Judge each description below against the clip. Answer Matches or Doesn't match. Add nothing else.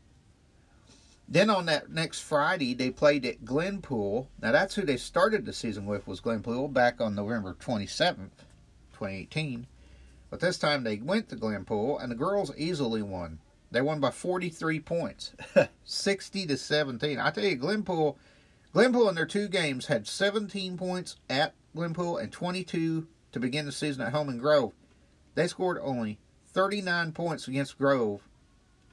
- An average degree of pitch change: Doesn't match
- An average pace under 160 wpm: Doesn't match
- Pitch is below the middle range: Doesn't match